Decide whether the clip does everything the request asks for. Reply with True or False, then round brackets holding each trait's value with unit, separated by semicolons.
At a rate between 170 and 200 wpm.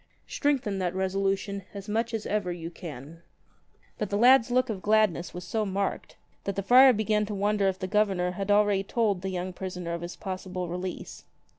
True (190 wpm)